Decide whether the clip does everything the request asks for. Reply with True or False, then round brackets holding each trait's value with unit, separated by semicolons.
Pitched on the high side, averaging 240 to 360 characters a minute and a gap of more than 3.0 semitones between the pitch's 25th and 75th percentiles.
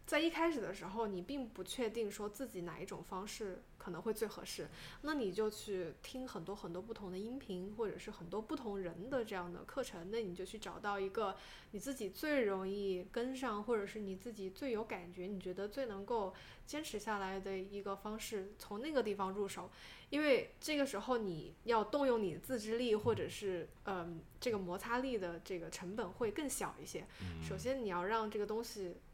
True (205 Hz; 300 characters per minute; 4.1 semitones)